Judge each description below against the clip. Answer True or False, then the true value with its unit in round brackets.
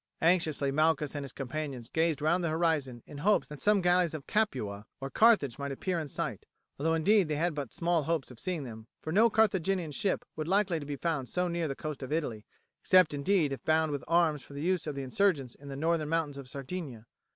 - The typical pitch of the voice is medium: True (155 Hz)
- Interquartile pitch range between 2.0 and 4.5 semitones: True (3.8 semitones)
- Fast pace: True (230 wpm)